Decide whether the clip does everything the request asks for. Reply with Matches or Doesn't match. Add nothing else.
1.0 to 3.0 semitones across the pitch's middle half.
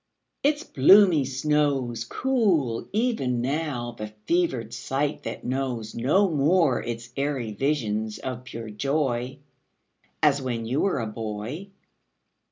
Doesn't match